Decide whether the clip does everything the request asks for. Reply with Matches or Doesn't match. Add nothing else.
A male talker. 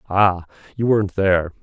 Matches